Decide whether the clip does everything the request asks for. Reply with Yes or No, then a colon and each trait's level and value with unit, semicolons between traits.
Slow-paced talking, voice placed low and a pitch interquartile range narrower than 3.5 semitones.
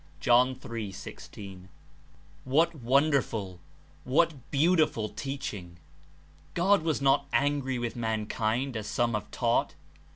No: slow, 110 wpm; low, 130 Hz; average, 4.6 semitones